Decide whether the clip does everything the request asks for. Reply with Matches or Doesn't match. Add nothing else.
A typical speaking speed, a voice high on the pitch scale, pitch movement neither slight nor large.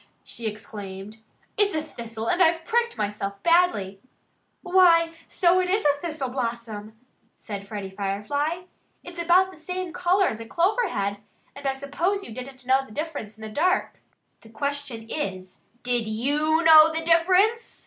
Doesn't match